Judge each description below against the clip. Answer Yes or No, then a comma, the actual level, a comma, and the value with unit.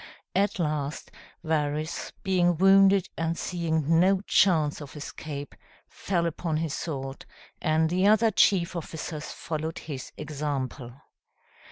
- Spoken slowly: Yes, slow, 120 wpm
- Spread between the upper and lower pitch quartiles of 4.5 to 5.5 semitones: No, average, 3.2 semitones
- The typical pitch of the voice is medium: Yes, medium, 160 Hz